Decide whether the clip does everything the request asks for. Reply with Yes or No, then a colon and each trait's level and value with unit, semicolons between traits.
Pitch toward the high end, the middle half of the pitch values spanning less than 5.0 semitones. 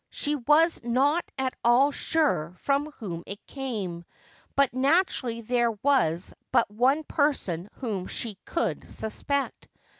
No: very high, 255 Hz; wide, 5.4 semitones